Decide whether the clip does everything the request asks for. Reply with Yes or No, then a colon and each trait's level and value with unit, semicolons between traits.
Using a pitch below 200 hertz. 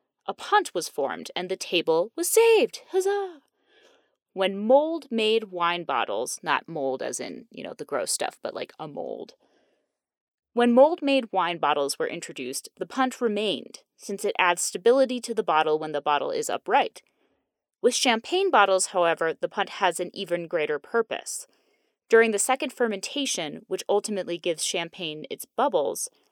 No: high, 210 Hz